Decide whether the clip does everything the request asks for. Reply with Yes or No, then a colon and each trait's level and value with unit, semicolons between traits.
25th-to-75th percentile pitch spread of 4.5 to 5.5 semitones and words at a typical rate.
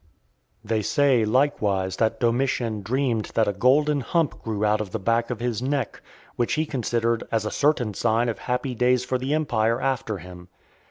No: average, 3.3 semitones; average, 180 wpm